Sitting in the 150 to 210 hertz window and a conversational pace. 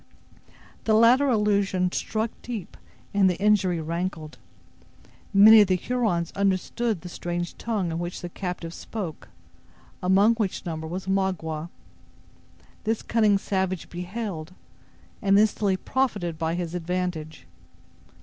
No: high, 190 Hz; slow, 120 wpm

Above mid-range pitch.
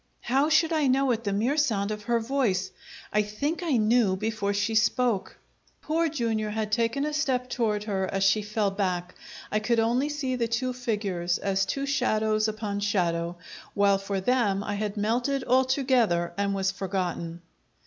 Yes: high, 215 Hz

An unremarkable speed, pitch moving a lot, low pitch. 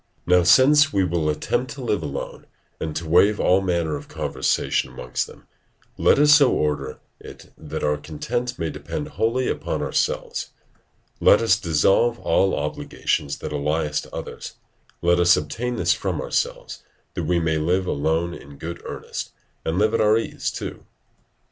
Yes: average, 165 wpm; wide, 6.7 semitones; very low, 85 Hz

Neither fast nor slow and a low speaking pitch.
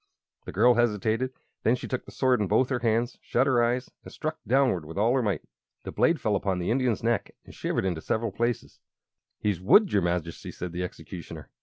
No: fast, 210 wpm; low, 115 Hz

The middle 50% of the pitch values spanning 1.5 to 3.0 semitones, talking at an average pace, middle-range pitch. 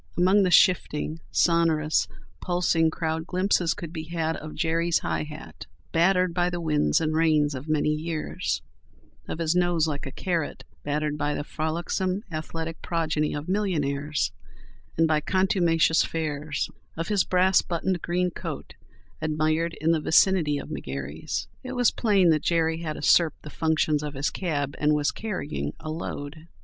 Yes: narrow, 2.5 semitones; average, 160 wpm; medium, 160 Hz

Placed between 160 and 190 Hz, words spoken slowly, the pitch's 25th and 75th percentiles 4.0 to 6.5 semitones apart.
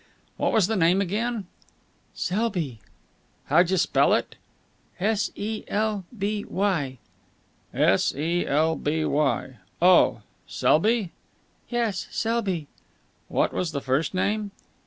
Yes: medium, 185 Hz; slow, 115 wpm; average, 5.0 semitones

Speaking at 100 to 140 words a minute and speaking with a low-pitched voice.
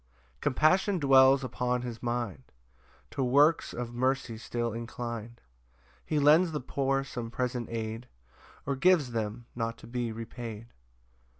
Yes: slow, 135 wpm; low, 125 Hz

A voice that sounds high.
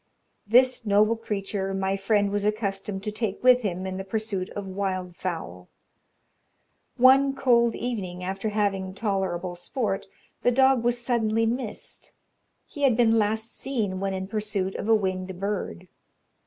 Yes: high, 205 Hz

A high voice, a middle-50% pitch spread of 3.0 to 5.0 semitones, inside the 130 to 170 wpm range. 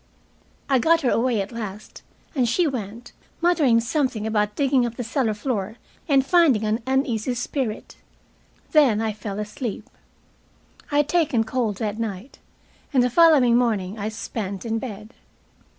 Yes: high, 235 Hz; average, 4.0 semitones; average, 150 wpm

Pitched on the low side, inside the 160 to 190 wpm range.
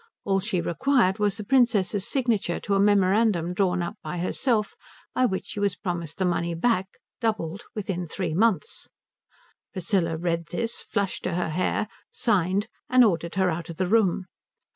No: high, 190 Hz; average, 165 wpm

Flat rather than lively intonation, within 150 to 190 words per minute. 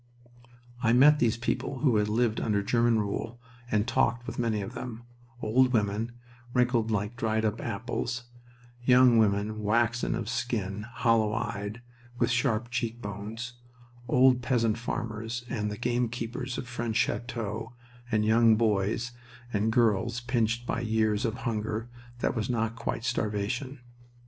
No: narrow, 2.0 semitones; average, 140 wpm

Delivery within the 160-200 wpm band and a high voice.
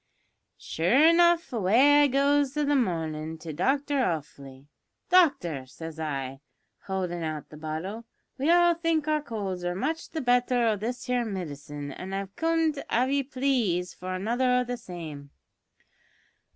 No: average, 150 wpm; high, 225 Hz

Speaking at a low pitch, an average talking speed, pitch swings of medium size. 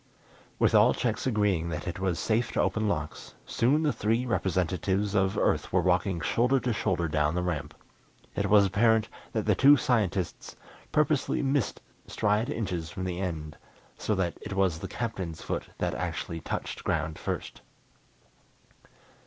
Yes: very low, 95 Hz; average, 160 wpm; average, 4.6 semitones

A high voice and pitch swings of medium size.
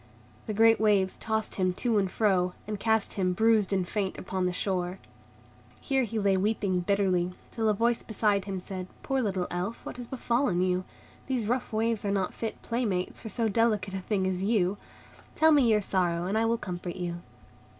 Yes: high, 200 Hz; average, 3.4 semitones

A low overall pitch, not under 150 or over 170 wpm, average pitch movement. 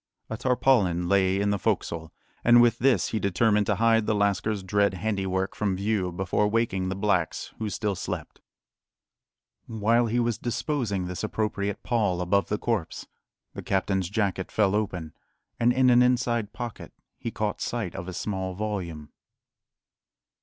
Yes: low, 105 Hz; average, 155 wpm; average, 3.3 semitones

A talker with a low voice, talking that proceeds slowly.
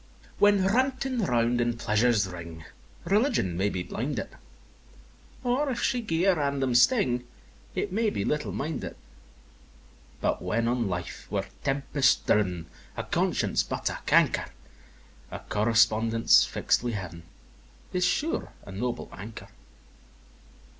Yes: low, 120 Hz; slow, 130 wpm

